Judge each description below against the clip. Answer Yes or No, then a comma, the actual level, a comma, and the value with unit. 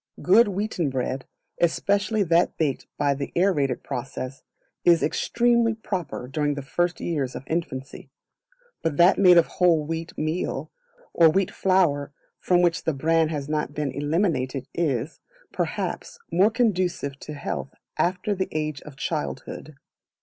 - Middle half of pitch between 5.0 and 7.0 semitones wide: No, average, 4.2 semitones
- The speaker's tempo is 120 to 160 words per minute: Yes, average, 140 wpm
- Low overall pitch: No, medium, 160 Hz